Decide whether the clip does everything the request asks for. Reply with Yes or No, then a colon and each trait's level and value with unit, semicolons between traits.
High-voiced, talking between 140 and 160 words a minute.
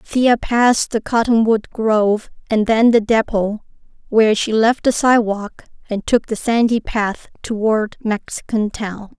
Yes: high, 220 Hz; average, 145 wpm